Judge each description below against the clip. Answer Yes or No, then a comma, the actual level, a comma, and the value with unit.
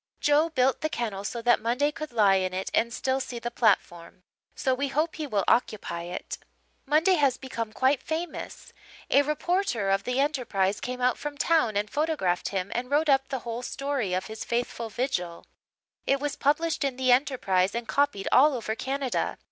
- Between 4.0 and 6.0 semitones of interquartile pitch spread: Yes, average, 5.0 semitones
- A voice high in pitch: Yes, very high, 250 Hz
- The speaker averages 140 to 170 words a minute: No, average, 190 wpm